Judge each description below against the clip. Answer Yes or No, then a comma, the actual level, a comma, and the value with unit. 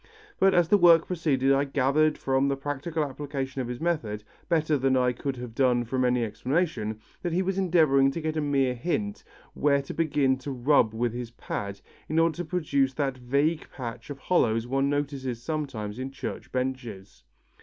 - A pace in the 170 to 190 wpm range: Yes, average, 185 wpm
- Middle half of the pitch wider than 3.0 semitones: Yes, average, 3.7 semitones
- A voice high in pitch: No, low, 135 Hz